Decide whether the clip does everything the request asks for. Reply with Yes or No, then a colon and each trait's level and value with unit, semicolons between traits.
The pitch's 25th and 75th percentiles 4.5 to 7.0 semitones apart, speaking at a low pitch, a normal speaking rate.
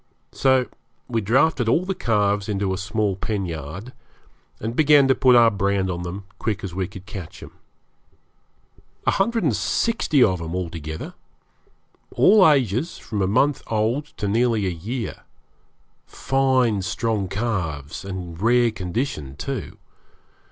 Yes: average, 5.2 semitones; low, 105 Hz; average, 150 wpm